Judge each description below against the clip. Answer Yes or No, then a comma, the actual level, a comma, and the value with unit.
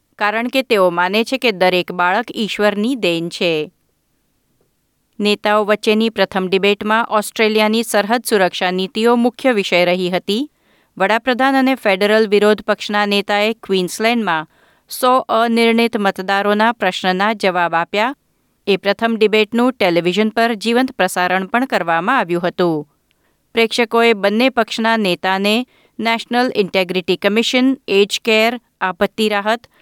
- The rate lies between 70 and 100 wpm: No, average, 115 wpm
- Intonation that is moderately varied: Yes, average, 3.4 semitones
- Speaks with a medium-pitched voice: No, high, 210 Hz